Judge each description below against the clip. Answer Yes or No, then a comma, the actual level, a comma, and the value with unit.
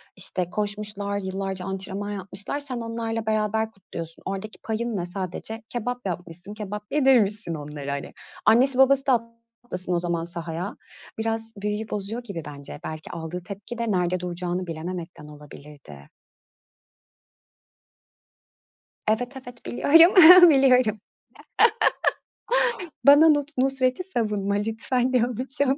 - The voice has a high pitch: Yes, high, 210 Hz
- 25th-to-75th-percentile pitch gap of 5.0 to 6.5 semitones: Yes, average, 5.3 semitones